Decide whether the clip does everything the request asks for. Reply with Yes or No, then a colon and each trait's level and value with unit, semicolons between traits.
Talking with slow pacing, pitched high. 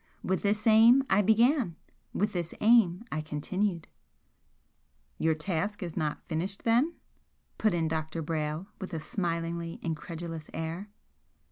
No: slow, 130 wpm; medium, 175 Hz